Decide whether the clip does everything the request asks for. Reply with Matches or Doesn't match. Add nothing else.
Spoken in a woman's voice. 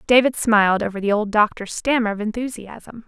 Matches